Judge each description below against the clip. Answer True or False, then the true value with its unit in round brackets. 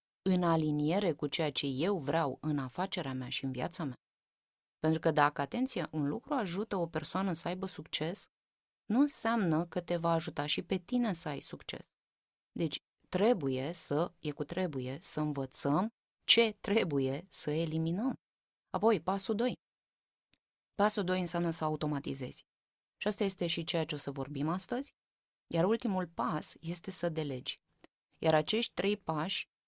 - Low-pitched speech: False (165 Hz)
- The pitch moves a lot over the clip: False (4.5 semitones)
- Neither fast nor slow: True (160 wpm)